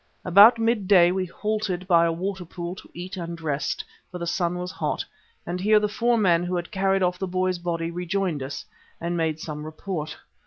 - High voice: No, medium, 180 Hz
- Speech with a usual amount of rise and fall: No, narrow, 2.3 semitones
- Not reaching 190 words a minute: No, average, 200 wpm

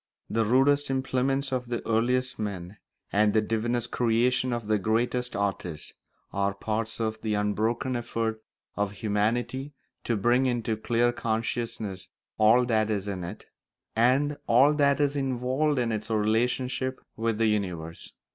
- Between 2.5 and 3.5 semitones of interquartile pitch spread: Yes, average, 2.9 semitones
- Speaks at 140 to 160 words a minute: Yes, average, 145 wpm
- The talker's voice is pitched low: Yes, low, 115 Hz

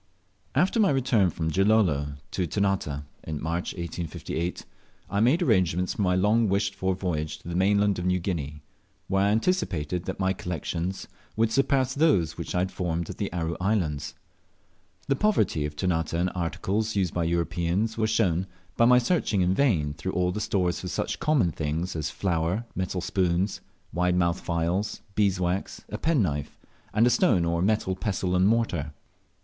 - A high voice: No, very low, 90 Hz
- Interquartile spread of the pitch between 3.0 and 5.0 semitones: Yes, average, 3.9 semitones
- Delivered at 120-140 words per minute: No, average, 170 wpm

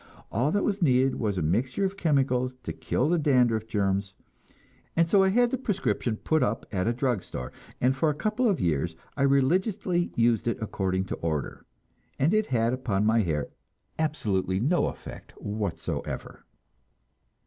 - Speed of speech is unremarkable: Yes, average, 170 wpm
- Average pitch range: No, wide, 8.2 semitones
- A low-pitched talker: Yes, low, 125 Hz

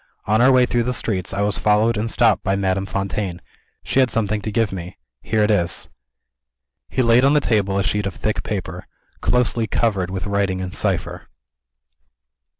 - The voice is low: Yes, low, 105 Hz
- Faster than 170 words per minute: Yes, average, 185 wpm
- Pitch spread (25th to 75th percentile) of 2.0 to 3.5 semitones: Yes, average, 3.0 semitones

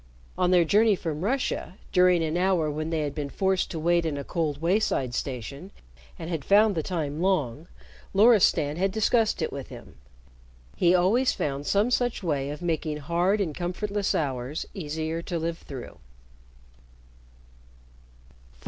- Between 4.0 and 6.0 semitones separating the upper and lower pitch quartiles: Yes, average, 4.3 semitones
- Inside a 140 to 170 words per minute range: Yes, average, 155 wpm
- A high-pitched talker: No, medium, 170 Hz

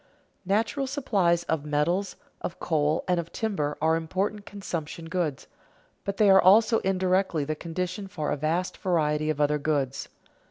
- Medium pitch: Yes, medium, 170 Hz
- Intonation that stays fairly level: No, average, 4.2 semitones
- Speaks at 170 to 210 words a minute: No, average, 155 wpm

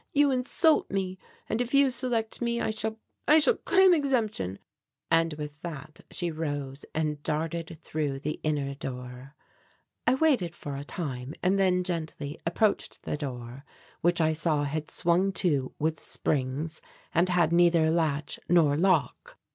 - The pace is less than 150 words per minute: No, average, 155 wpm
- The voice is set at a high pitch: No, medium, 165 Hz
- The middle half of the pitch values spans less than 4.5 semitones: No, average, 5.0 semitones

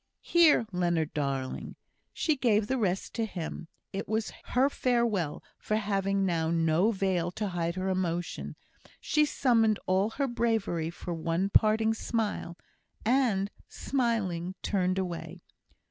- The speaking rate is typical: No, slow, 130 wpm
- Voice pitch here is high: Yes, high, 195 Hz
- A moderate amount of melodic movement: Yes, average, 4.6 semitones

